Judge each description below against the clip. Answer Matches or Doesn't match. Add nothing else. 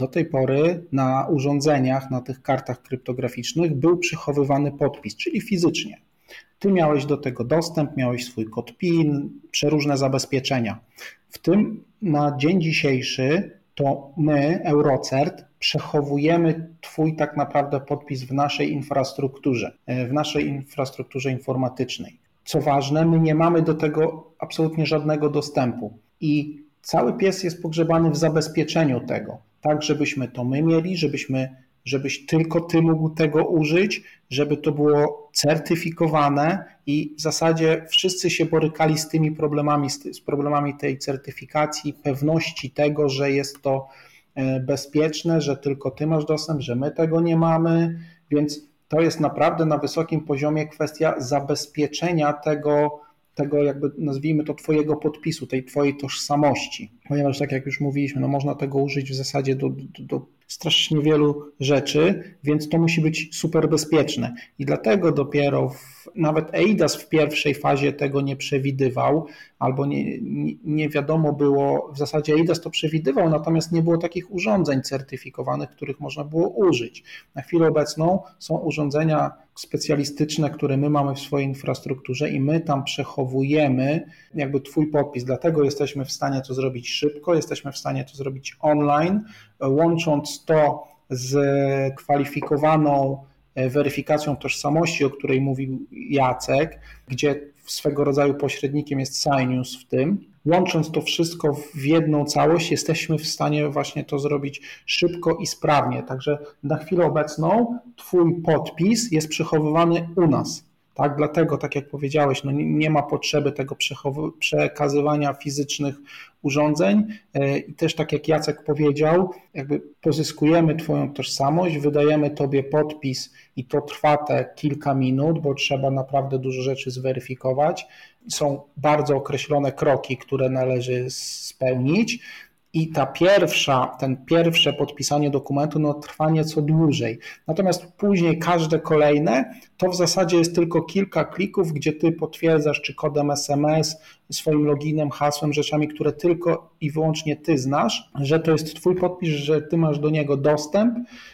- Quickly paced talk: Doesn't match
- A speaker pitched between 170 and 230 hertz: Doesn't match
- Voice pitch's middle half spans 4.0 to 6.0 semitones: Doesn't match